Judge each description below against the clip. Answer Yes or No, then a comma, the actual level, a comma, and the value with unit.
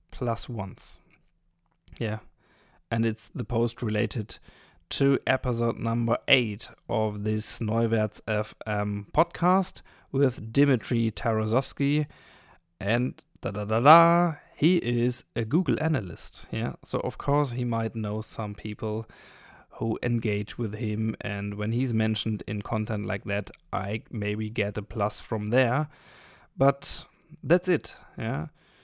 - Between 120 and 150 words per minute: Yes, average, 130 wpm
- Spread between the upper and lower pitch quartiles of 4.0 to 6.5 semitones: No, average, 3.6 semitones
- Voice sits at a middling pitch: No, low, 115 Hz